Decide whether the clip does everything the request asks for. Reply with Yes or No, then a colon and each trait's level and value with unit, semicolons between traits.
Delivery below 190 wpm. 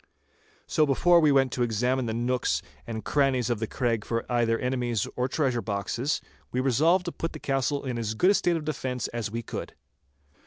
No: average, 200 wpm